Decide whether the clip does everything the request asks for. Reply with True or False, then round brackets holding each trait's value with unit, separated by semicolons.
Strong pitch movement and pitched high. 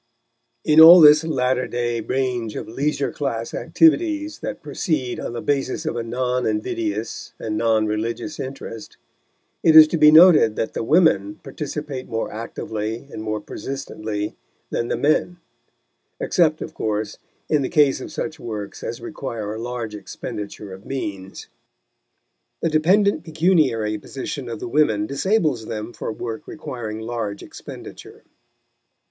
False (5.8 semitones; 125 Hz)